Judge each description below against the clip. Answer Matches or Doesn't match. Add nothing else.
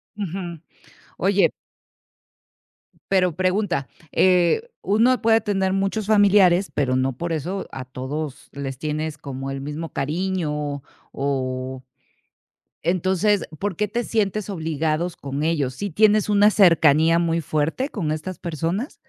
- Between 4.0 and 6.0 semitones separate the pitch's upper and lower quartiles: Matches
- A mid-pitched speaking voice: Matches